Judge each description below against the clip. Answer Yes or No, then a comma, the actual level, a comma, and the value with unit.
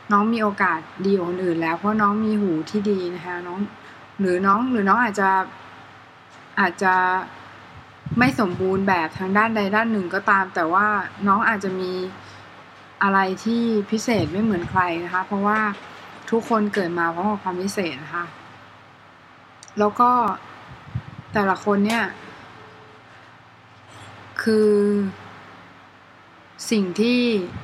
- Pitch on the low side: No, high, 195 Hz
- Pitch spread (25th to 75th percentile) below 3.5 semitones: Yes, average, 2.9 semitones